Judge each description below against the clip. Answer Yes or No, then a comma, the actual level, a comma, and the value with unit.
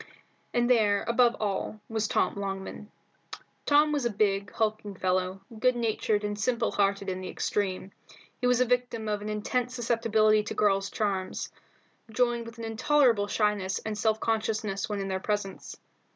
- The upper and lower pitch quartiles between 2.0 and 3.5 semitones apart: Yes, average, 2.8 semitones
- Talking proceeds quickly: No, average, 165 wpm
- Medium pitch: No, high, 215 Hz